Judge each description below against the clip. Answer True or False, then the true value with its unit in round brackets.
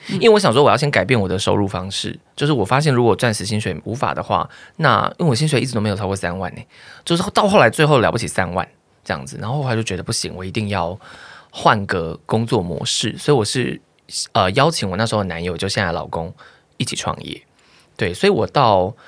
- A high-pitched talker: False (110 Hz)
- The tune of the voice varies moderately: False (7.3 semitones)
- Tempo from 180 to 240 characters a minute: False (350 characters per minute)